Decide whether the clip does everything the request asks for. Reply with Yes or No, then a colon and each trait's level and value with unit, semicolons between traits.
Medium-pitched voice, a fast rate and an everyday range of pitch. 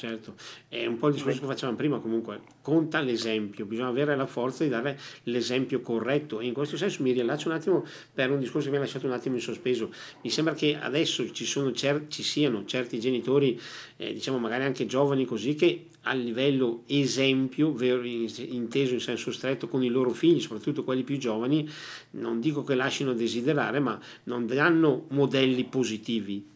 No: low, 130 Hz; fast, 185 wpm; average, 3.1 semitones